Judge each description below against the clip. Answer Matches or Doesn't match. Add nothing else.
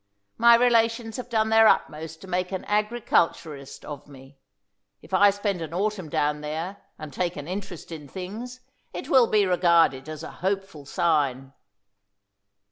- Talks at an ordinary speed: Matches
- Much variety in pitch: Matches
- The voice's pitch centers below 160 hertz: Doesn't match